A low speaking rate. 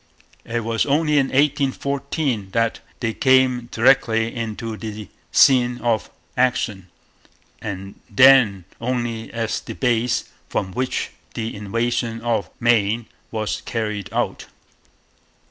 Yes: slow, 110 wpm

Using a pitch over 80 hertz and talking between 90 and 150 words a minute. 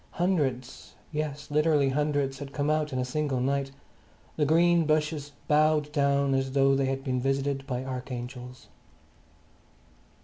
Yes: medium, 140 Hz; average, 140 wpm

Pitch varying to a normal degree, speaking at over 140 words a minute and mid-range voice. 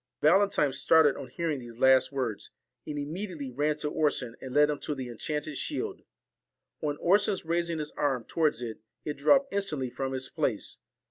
Yes: average, 3.7 semitones; average, 175 wpm; medium, 150 Hz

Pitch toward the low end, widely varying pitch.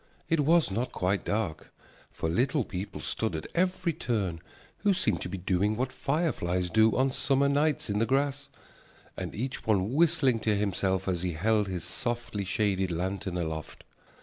Yes: low, 110 Hz; wide, 6.6 semitones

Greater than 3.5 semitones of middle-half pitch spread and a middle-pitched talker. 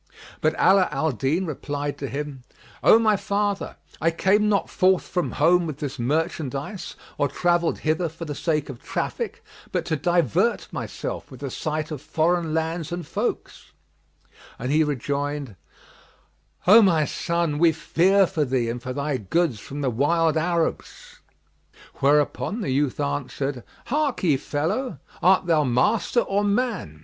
Yes: average, 4.0 semitones; medium, 160 Hz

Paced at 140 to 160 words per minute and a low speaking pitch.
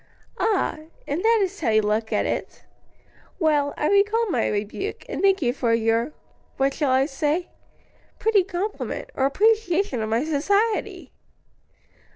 No: average, 150 wpm; very high, 310 Hz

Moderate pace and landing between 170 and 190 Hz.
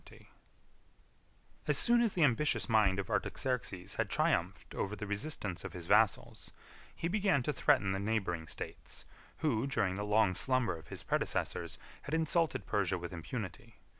No: average, 160 wpm; low, 110 Hz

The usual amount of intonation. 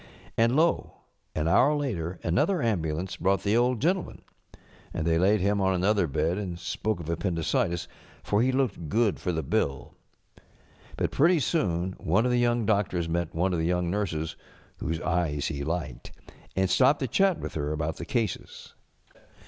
No: wide, 5.9 semitones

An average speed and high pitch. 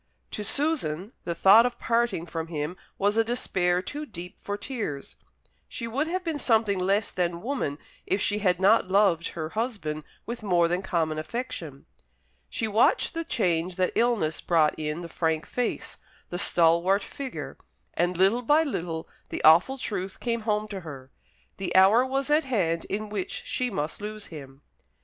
Yes: average, 170 wpm; high, 195 Hz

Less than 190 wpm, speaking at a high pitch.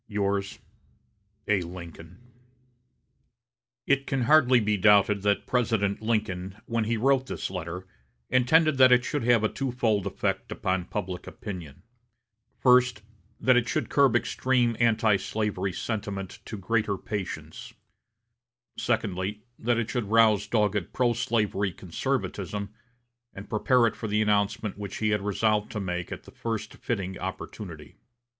No: slow, 135 wpm; low, 105 Hz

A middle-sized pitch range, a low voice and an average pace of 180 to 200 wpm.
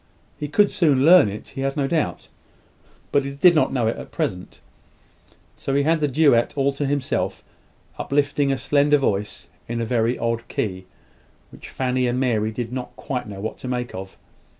Yes: average, 3.6 semitones; low, 130 Hz; average, 190 wpm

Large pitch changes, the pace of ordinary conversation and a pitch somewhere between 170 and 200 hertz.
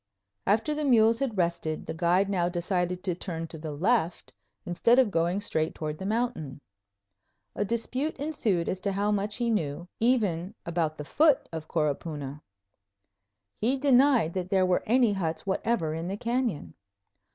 Yes: wide, 5.8 semitones; average, 165 wpm; high, 190 Hz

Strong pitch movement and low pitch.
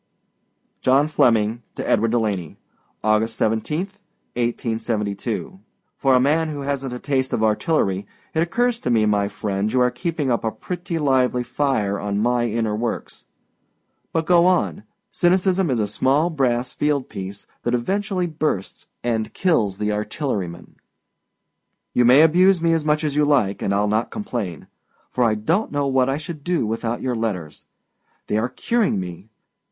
Yes: wide, 6.4 semitones; low, 125 Hz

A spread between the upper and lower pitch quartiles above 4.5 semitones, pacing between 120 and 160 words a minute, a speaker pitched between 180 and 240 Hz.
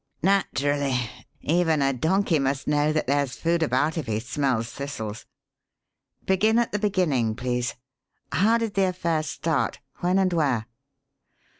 No: wide, 5.6 semitones; average, 140 wpm; medium, 150 Hz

